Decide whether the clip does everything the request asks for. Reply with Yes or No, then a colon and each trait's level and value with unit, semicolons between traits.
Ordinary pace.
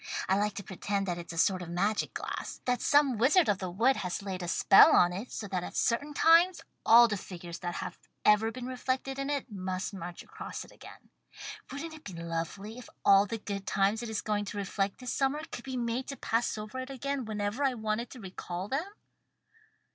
No: fast, 220 wpm